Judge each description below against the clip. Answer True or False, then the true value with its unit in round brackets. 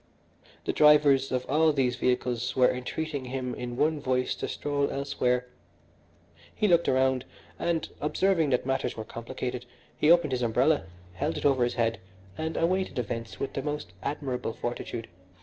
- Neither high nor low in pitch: False (130 Hz)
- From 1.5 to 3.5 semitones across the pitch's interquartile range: True (3.2 semitones)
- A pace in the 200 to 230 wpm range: False (160 wpm)